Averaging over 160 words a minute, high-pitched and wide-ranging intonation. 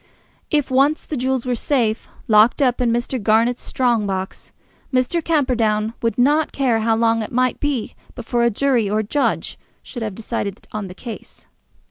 No: average, 175 wpm; high, 240 Hz; average, 3.2 semitones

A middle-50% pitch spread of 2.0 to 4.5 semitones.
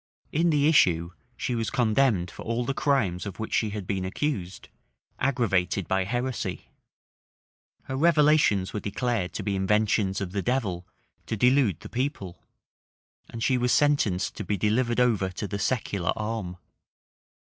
No: average, 5.1 semitones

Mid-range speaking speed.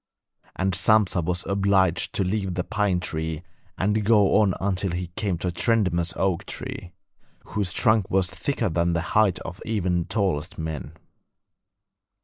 Yes: average, 155 wpm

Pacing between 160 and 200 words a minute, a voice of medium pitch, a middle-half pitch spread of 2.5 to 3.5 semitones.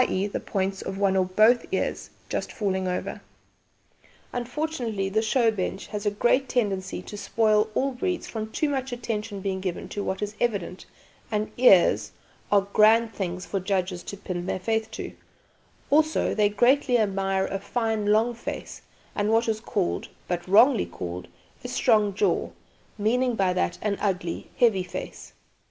No: average, 165 wpm; high, 210 Hz; average, 3.2 semitones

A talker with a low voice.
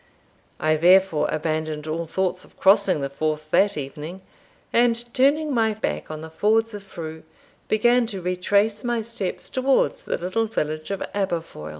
No: high, 190 Hz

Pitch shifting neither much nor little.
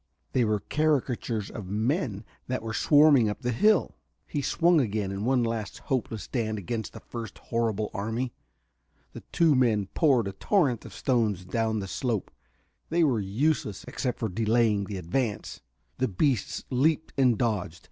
Yes: average, 4.0 semitones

